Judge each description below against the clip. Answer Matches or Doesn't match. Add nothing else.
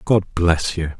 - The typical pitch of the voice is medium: Doesn't match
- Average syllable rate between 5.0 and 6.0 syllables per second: Doesn't match